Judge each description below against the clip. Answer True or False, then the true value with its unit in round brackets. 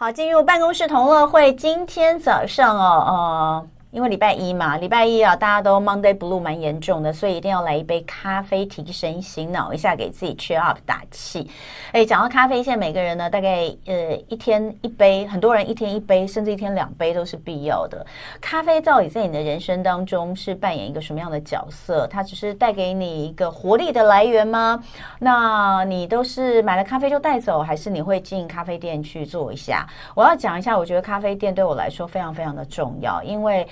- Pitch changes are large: False (4.7 semitones)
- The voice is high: True (195 Hz)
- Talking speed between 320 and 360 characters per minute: True (340 characters per minute)